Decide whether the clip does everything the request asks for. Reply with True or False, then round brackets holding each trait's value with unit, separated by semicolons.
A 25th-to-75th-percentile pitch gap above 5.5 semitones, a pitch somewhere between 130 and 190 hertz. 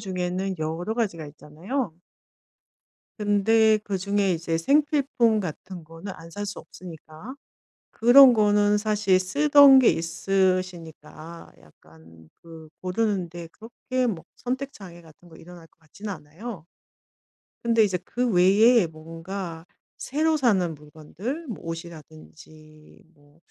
False (5.2 semitones; 185 Hz)